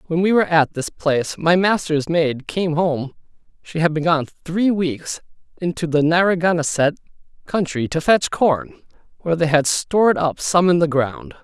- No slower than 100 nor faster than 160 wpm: No, average, 175 wpm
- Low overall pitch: No, medium, 165 Hz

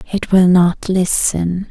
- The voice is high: No, medium, 180 Hz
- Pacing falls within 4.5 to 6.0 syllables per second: No, 3.5 syllables/s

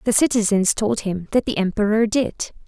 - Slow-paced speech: No, average, 180 wpm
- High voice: Yes, high, 210 Hz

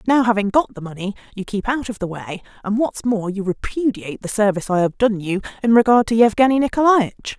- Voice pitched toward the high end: Yes, high, 215 Hz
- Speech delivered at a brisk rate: Yes, fast, 220 wpm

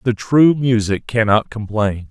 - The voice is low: Yes, low, 115 Hz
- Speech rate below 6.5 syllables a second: Yes, 4.0 syllables/s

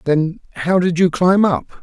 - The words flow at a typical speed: Yes, average, 195 wpm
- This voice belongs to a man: Yes, male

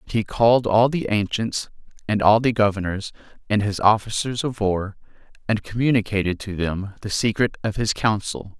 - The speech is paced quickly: No, average, 165 wpm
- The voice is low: Yes, low, 105 Hz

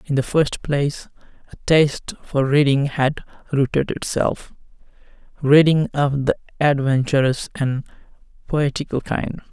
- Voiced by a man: Yes, male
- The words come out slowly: Yes, slow, 105 wpm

